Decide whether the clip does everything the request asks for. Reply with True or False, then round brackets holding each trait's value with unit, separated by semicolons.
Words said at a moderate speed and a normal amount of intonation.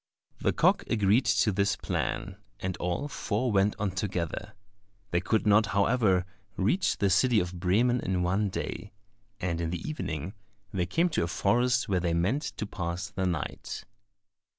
True (165 wpm; 3.7 semitones)